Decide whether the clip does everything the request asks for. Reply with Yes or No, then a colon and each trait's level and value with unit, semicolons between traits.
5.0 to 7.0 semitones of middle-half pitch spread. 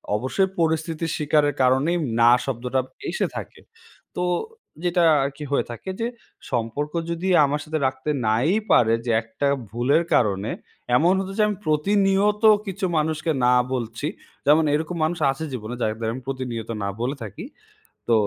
Yes: wide, 5.4 semitones